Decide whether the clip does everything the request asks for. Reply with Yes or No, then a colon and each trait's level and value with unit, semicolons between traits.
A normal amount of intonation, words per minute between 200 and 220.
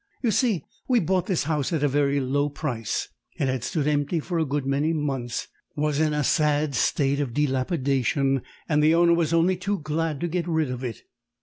Yes: average, 3.0 semitones; fast, 205 wpm